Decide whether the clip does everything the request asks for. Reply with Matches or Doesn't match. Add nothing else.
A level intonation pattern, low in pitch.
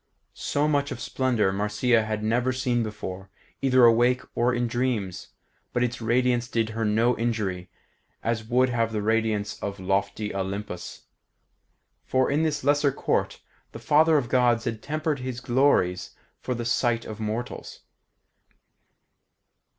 Doesn't match